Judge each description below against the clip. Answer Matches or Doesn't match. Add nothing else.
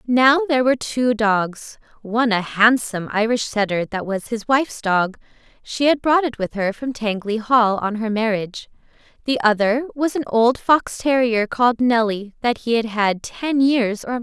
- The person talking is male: Doesn't match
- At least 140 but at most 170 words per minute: Doesn't match